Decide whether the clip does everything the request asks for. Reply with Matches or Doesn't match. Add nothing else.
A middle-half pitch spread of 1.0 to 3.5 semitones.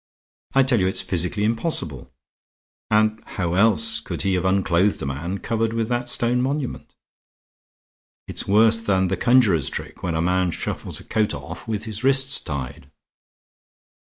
Doesn't match